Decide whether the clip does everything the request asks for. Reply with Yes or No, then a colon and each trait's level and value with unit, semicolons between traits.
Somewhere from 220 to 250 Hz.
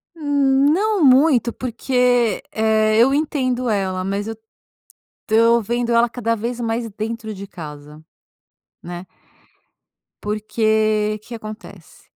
Yes: high, 230 Hz